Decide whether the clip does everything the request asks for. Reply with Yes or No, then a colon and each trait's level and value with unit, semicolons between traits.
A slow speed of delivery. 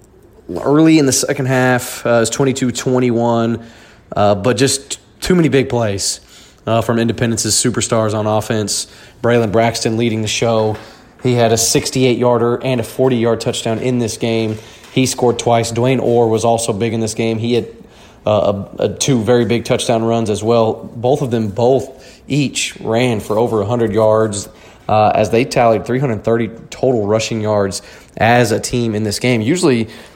No: average, 180 wpm